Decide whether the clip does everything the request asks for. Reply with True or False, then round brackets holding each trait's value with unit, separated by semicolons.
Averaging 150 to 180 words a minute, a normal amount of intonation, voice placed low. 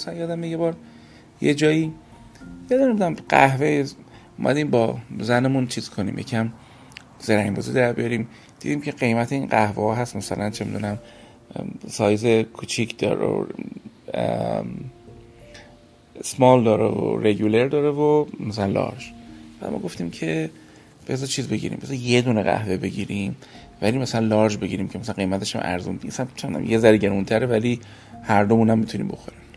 True (155 wpm; 3.6 semitones; 115 Hz)